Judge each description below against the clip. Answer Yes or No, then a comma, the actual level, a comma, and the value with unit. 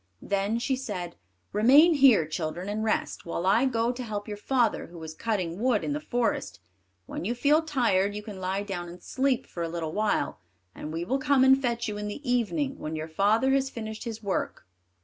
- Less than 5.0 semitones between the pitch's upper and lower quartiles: No, wide, 5.5 semitones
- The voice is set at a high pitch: Yes, high, 215 Hz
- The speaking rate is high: Yes, fast, 210 wpm